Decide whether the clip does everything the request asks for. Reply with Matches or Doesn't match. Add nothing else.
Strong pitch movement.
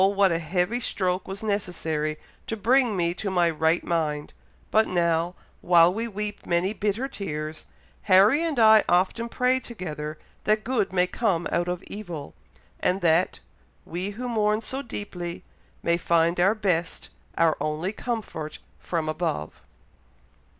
Doesn't match